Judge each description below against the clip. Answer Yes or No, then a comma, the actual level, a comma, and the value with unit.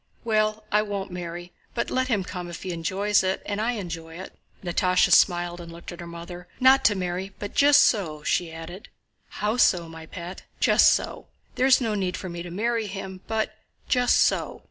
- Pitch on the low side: No, medium, 185 Hz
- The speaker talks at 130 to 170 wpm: No, average, 195 wpm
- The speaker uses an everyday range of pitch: Yes, average, 3.6 semitones